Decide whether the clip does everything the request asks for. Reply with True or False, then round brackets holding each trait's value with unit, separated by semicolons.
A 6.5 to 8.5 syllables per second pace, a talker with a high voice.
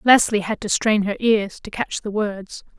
False (4.4 syllables/s; 210 Hz)